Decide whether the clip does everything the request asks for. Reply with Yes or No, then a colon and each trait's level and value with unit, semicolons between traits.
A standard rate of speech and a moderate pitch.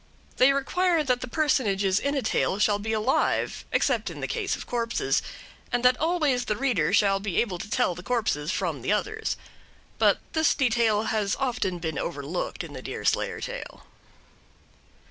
No: average, 170 wpm; high, 225 Hz